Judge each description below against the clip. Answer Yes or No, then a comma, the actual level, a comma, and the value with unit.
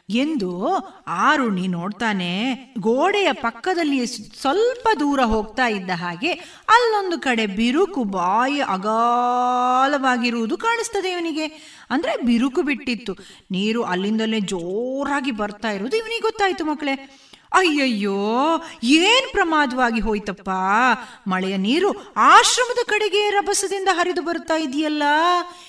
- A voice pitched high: Yes, very high, 270 Hz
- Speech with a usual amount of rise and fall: No, wide, 8.0 semitones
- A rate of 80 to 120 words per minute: Yes, average, 95 wpm